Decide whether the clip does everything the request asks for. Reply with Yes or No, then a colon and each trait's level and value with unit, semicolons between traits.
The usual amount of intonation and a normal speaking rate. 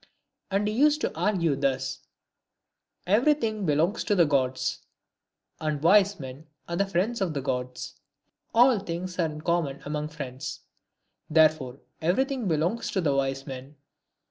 No: wide, 6.3 semitones; average, 145 wpm